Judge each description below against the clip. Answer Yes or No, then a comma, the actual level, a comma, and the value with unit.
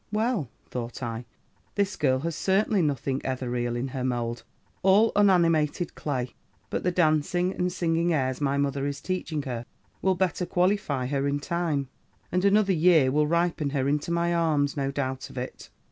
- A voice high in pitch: No, medium, 150 Hz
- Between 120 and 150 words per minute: No, average, 170 wpm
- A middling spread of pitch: Yes, average, 5.0 semitones